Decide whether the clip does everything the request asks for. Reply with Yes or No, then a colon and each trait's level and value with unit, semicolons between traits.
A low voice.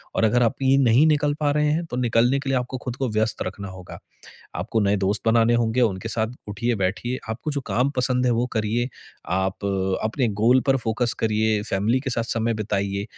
Yes: low, 115 Hz